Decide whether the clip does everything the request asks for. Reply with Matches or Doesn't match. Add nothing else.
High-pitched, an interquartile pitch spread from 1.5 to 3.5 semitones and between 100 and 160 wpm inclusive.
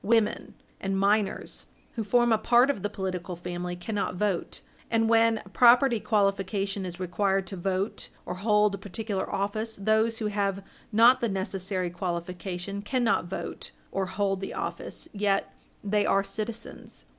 Matches